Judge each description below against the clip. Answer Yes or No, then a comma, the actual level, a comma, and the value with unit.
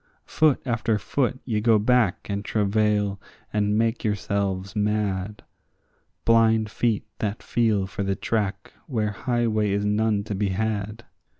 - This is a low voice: Yes, low, 105 Hz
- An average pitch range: No, narrow, 1.9 semitones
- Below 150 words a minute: Yes, slow, 135 wpm